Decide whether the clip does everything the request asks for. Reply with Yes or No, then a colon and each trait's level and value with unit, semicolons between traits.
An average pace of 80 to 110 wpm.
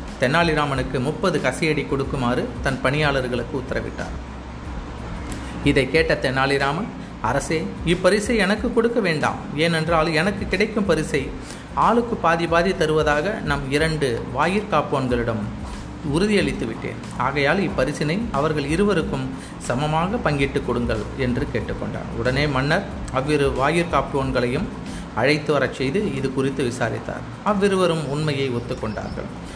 Yes: average, 105 wpm